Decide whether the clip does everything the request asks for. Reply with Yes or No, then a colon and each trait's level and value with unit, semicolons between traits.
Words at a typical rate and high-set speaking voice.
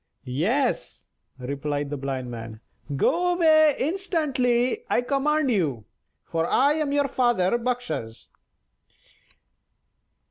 No: slow, 100 wpm; high, 245 Hz